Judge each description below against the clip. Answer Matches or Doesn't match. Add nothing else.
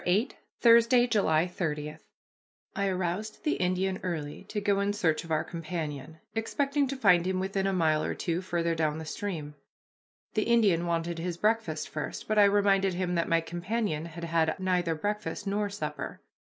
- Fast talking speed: Doesn't match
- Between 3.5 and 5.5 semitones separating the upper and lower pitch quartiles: Matches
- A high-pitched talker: Doesn't match